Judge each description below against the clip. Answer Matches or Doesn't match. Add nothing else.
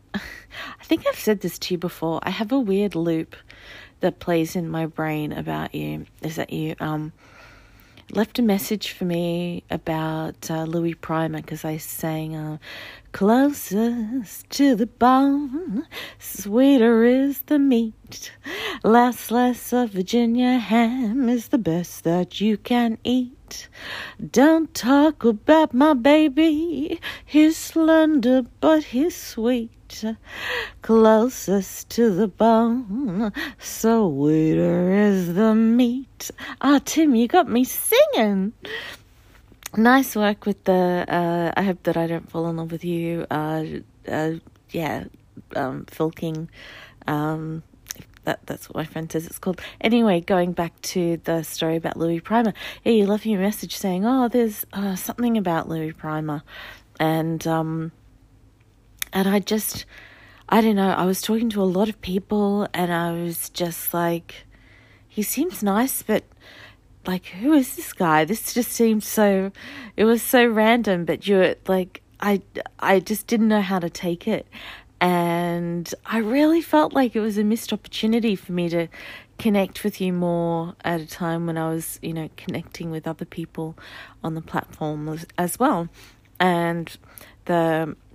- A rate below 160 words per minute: Matches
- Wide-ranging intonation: Matches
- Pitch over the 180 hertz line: Matches